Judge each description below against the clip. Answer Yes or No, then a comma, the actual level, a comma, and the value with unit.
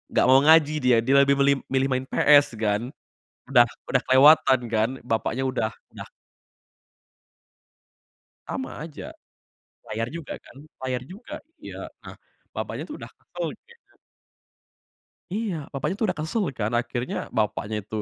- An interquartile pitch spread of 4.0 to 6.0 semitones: Yes, average, 4.5 semitones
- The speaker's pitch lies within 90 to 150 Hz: Yes, low, 135 Hz